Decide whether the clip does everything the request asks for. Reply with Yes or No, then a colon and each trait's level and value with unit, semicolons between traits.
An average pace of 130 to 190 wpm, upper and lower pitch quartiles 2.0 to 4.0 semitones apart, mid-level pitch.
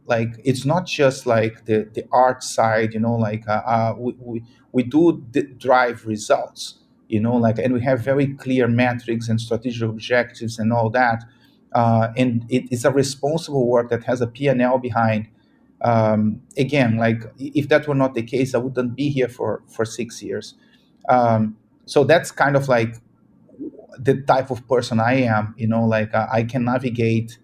No: average, 185 wpm; narrow, 2.5 semitones; low, 120 Hz